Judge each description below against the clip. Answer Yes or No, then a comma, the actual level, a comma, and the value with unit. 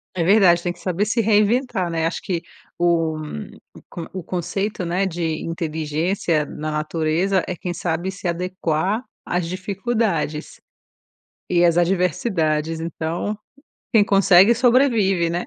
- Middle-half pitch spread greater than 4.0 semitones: No, average, 3.1 semitones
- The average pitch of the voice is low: No, medium, 175 Hz